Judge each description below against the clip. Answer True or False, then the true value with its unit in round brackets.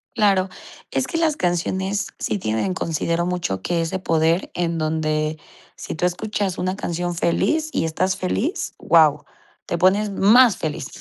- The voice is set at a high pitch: False (175 Hz)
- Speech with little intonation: False (3.2 semitones)